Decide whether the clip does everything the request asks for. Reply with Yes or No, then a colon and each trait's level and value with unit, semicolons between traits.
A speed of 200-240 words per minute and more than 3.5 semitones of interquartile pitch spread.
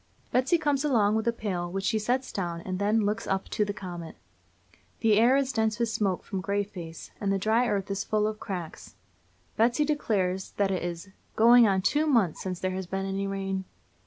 No: fast, 205 wpm; average, 3.2 semitones